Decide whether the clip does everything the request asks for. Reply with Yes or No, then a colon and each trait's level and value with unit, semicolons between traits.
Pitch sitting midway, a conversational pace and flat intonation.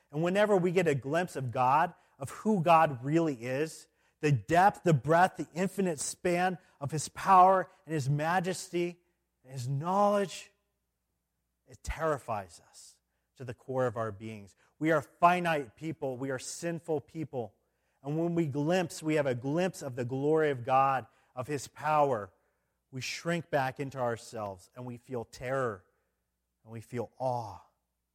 No: medium, 145 Hz; average, 160 wpm; wide, 5.5 semitones